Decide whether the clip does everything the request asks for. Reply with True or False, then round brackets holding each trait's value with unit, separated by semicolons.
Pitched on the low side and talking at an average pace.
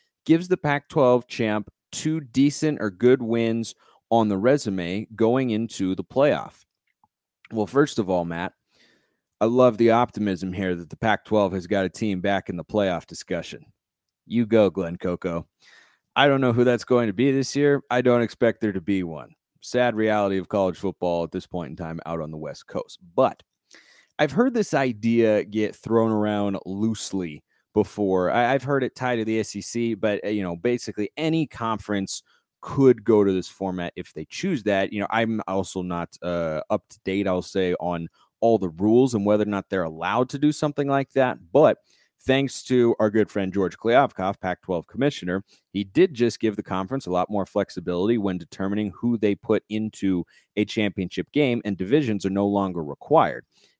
True (105 Hz; 190 wpm)